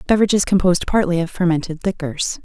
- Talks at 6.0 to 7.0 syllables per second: Yes, 6.6 syllables/s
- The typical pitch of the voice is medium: Yes, medium, 180 Hz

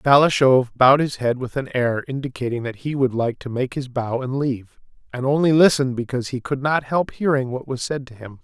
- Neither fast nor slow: No, fast, 230 wpm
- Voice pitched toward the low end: Yes, low, 130 Hz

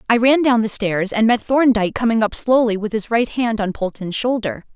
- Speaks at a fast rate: Yes, fast, 225 wpm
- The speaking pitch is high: Yes, high, 225 Hz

